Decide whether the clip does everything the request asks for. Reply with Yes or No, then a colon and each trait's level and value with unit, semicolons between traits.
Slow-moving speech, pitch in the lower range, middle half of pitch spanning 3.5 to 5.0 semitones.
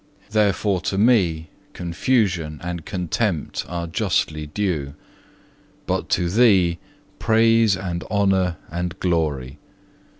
Yes: slow, 100 wpm; very low, 90 Hz; average, 3.8 semitones